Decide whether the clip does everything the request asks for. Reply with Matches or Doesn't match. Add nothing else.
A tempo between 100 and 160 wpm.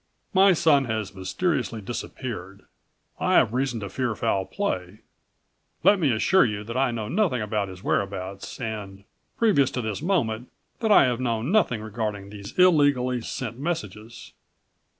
Matches